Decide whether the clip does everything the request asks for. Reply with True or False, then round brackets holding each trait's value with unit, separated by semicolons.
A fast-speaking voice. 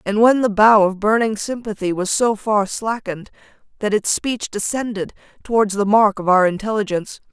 False (170 wpm)